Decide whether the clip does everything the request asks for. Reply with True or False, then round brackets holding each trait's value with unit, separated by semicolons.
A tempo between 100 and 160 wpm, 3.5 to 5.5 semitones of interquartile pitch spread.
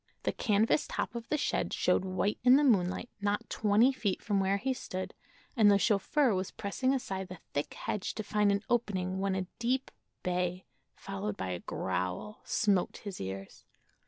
False (180 wpm; 3.9 semitones)